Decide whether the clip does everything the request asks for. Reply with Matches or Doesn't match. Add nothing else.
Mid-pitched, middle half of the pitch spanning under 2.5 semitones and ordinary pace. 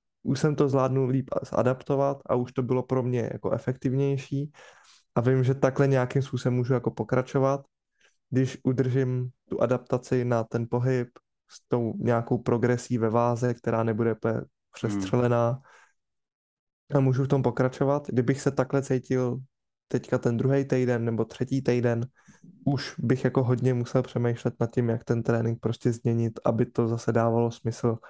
Doesn't match